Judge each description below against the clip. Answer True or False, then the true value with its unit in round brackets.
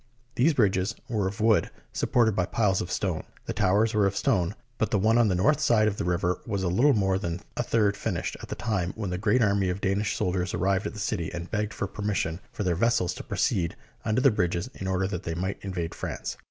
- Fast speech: True (235 wpm)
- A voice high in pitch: False (100 Hz)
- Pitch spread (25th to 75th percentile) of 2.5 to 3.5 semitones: True (3.1 semitones)